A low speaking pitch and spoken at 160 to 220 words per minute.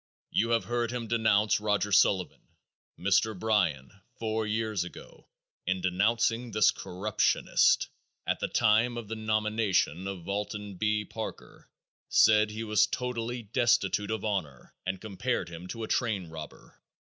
No: low, 105 Hz; average, 140 wpm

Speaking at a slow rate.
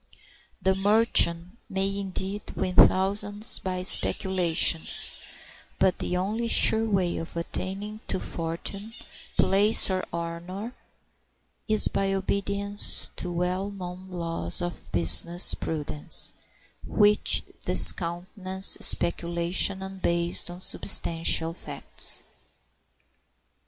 Yes: slow, 95 wpm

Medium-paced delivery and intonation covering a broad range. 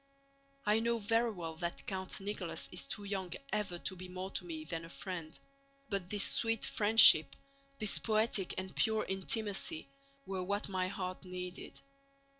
No: average, 160 wpm; average, 2.8 semitones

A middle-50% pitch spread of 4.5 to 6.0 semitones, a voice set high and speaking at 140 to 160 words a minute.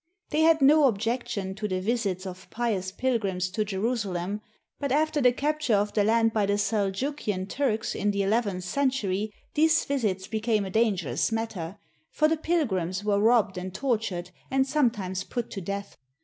No: average, 4.8 semitones; high, 215 Hz; average, 175 wpm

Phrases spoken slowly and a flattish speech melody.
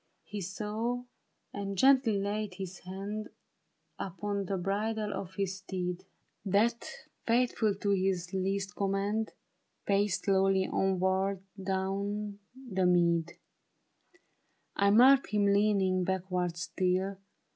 Yes: slow, 115 wpm; narrow, 1.8 semitones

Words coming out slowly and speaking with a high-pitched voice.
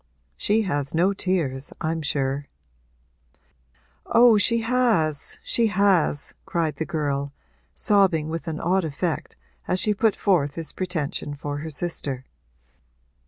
No: slow, 125 wpm; medium, 165 Hz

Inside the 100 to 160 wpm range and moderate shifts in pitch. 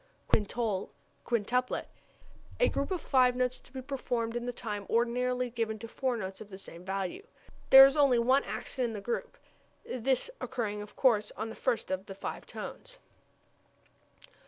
No: average, 170 wpm; average, 3.4 semitones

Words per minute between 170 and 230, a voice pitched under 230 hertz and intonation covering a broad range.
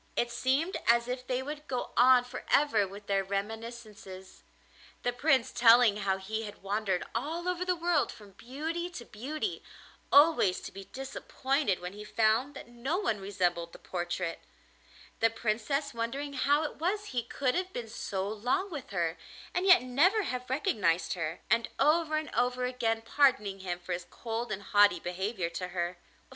No: average, 175 wpm; high, 235 Hz; wide, 6.1 semitones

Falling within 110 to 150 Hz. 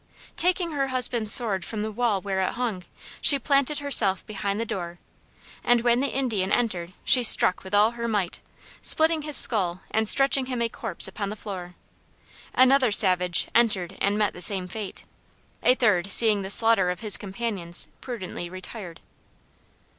No: high, 215 Hz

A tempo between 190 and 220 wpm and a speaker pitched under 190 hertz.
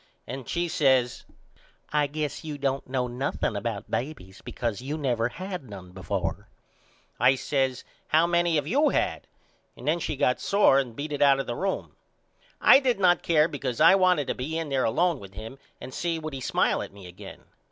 Yes: average, 195 wpm; medium, 140 Hz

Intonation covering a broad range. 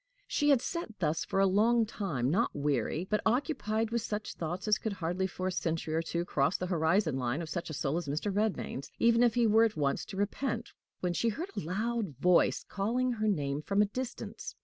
Yes: wide, 5.7 semitones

